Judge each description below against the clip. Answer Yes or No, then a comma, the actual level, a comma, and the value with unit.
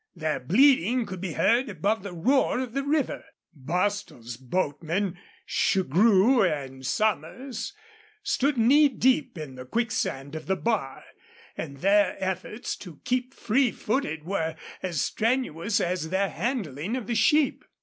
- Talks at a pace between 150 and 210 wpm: No, average, 140 wpm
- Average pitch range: No, wide, 7.3 semitones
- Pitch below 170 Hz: No, high, 200 Hz